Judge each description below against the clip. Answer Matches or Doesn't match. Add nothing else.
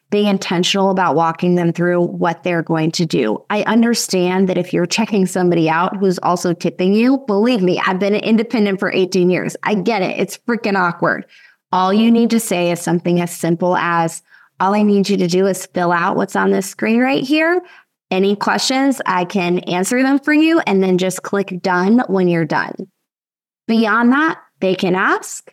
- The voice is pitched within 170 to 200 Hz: Matches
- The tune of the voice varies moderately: Matches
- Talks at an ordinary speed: Matches